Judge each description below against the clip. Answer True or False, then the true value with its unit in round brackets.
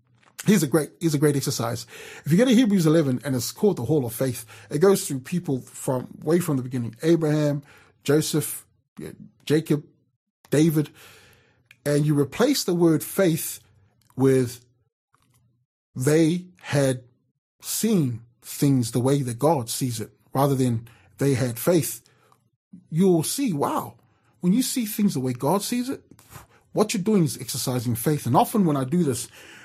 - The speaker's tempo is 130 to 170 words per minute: True (160 wpm)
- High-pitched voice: False (140 Hz)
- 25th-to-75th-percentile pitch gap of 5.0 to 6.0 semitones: True (5.3 semitones)